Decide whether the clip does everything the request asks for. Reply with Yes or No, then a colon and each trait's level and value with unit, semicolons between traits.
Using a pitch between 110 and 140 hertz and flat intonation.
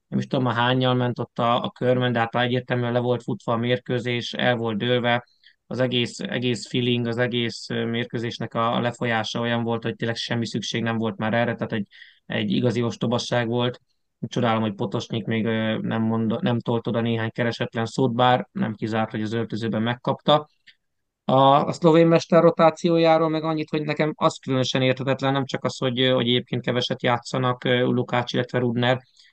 Yes: low, 120 Hz; narrow, 1.8 semitones